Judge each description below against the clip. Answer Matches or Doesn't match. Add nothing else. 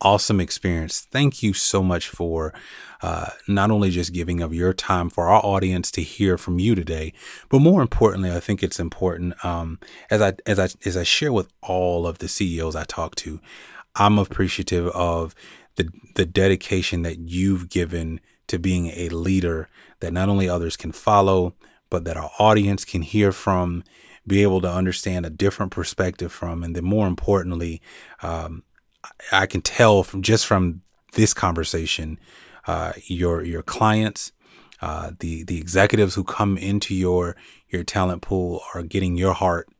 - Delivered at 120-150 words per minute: Doesn't match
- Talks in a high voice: Doesn't match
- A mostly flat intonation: Matches